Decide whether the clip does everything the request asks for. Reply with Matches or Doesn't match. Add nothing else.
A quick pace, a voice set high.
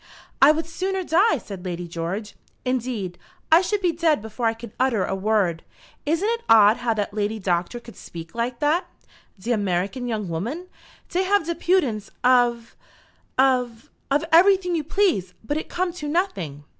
Doesn't match